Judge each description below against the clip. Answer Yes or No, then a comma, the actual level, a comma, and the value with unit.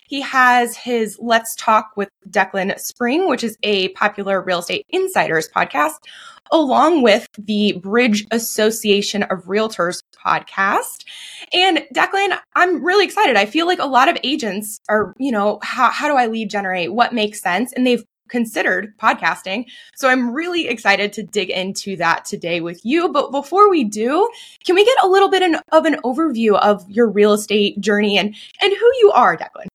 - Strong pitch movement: Yes, wide, 7.7 semitones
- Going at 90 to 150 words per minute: No, average, 175 wpm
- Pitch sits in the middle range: No, high, 230 Hz